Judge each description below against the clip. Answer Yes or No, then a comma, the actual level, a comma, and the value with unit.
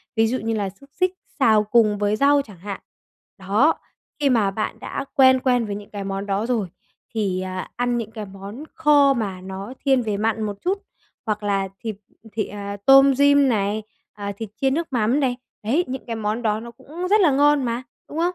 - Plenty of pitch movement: No, average, 4.9 semitones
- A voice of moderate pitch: No, high, 225 Hz